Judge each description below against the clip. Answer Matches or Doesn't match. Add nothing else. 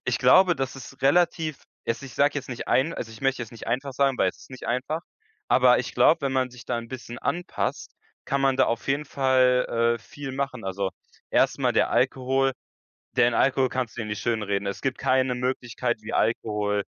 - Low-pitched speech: Matches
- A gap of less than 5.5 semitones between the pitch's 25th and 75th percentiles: Matches